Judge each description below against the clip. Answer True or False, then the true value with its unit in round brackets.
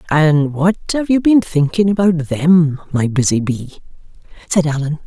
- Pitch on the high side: False (165 Hz)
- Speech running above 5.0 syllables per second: False (4.4 syllables/s)